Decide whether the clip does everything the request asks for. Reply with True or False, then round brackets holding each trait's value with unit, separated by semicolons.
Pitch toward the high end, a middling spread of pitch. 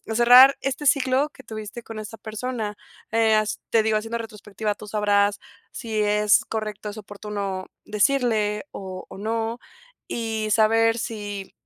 False (215 Hz; 1.7 semitones)